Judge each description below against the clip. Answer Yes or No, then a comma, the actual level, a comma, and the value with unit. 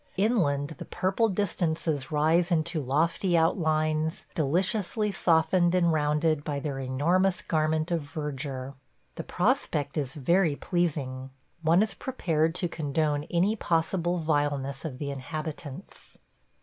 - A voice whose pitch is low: No, medium, 160 Hz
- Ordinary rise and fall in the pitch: Yes, average, 3.2 semitones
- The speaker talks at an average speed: No, slow, 125 wpm